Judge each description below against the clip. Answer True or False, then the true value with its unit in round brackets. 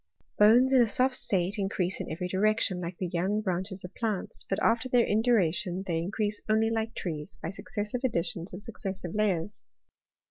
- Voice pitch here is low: False (200 Hz)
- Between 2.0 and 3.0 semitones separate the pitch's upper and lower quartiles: False (3.6 semitones)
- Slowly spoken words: False (185 wpm)